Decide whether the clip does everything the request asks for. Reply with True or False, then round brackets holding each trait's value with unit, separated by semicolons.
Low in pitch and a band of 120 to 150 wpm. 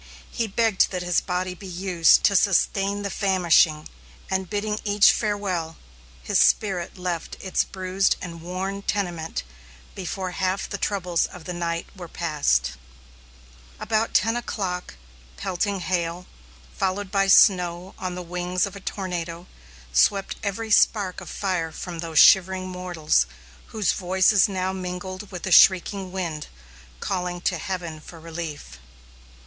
False (185 Hz; 140 wpm)